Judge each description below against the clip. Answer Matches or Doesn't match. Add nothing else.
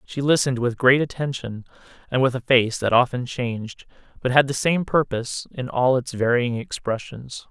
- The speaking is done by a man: Matches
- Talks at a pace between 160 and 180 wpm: Matches